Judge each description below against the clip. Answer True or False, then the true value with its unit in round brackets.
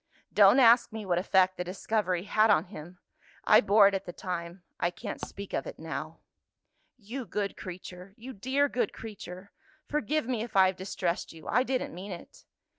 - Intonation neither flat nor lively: True (3.7 semitones)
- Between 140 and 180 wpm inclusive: False (190 wpm)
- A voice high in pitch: True (200 Hz)